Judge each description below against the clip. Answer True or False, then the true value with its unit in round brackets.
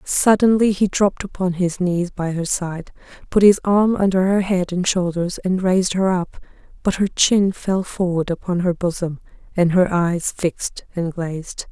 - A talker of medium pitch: True (180 Hz)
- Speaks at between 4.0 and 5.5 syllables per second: True (4.5 syllables/s)